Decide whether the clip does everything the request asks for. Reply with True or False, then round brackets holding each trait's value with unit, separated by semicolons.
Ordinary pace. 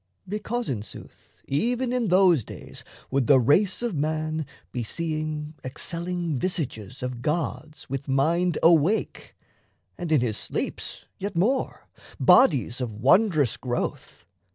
False (130 wpm)